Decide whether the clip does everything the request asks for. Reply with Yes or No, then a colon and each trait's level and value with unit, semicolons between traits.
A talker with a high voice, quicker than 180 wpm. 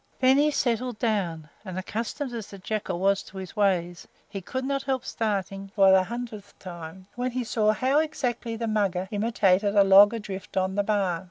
Yes: high, 205 Hz; average, 190 wpm